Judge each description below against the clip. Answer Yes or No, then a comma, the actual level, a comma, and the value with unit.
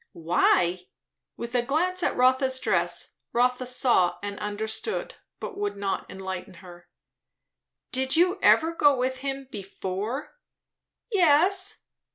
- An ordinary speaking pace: No, slow, 125 wpm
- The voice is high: Yes, very high, 255 Hz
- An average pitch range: No, wide, 7.2 semitones